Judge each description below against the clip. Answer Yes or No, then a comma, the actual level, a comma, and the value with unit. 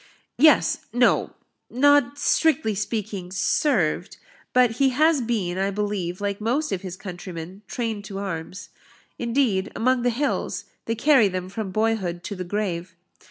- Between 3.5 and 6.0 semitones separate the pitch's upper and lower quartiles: Yes, average, 4.8 semitones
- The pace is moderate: Yes, average, 145 wpm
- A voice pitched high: Yes, high, 210 Hz